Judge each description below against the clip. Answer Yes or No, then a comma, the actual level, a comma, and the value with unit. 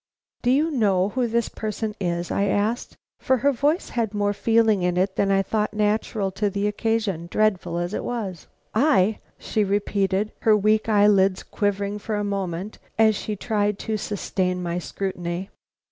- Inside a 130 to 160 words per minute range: No, average, 170 wpm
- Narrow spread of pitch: Yes, narrow, 2.3 semitones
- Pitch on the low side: No, high, 205 Hz